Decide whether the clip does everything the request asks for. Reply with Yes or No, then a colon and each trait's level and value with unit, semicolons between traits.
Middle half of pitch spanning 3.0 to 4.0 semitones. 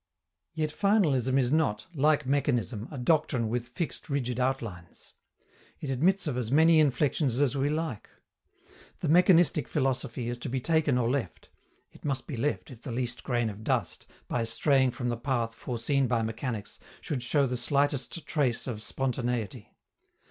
Yes: average, 3.4 semitones